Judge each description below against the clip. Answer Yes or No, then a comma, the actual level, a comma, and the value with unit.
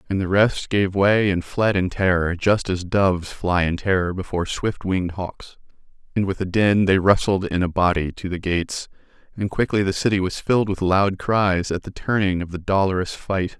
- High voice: No, very low, 95 Hz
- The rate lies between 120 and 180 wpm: No, fast, 205 wpm